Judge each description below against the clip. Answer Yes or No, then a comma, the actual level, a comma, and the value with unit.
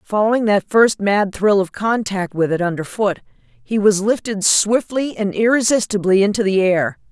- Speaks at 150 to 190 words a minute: Yes, average, 160 wpm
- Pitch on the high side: Yes, high, 205 Hz